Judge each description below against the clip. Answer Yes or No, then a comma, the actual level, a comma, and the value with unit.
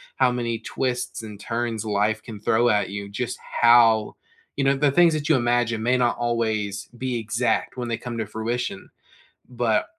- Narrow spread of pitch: Yes, narrow, 2.0 semitones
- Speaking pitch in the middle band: No, low, 120 Hz